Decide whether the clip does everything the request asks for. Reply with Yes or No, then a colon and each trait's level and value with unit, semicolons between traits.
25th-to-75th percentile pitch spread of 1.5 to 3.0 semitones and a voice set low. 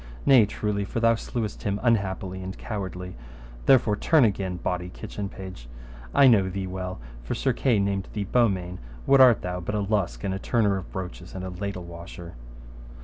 Yes: narrow, 2.6 semitones; very low, 95 Hz